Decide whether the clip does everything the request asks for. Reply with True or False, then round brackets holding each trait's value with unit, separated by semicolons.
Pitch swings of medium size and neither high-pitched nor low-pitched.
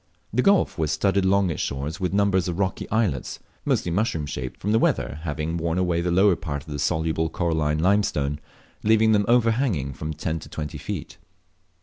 False (4.6 semitones; 85 Hz)